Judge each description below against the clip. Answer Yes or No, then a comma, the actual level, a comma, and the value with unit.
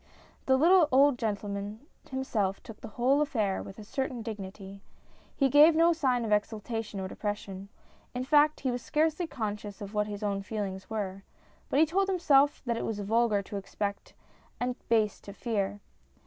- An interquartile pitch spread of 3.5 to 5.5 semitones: Yes, average, 5.0 semitones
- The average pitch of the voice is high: Yes, high, 225 Hz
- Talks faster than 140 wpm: Yes, average, 175 wpm